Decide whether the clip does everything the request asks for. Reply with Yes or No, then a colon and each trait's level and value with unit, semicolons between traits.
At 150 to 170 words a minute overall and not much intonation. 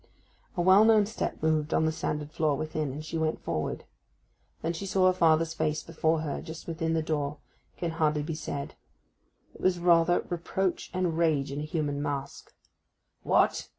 No: average, 180 wpm; narrow, 2.1 semitones